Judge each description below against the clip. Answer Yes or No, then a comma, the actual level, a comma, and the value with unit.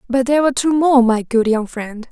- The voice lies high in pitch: Yes, very high, 250 Hz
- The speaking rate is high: Yes, fast, 255 wpm